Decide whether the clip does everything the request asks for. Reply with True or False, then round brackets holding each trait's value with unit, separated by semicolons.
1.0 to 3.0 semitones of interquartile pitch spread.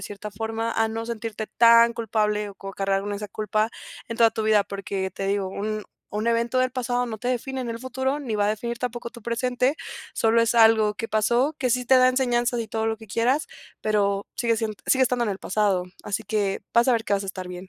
True (2.4 semitones)